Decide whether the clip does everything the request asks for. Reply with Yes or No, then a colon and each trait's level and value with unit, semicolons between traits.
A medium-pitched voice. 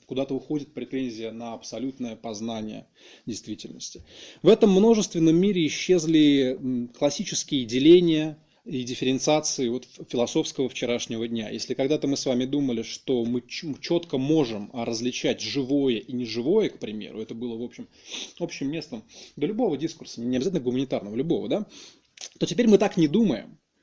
No: low, 130 Hz